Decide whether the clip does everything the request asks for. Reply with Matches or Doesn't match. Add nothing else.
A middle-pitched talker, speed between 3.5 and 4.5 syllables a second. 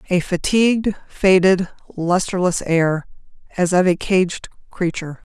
Matches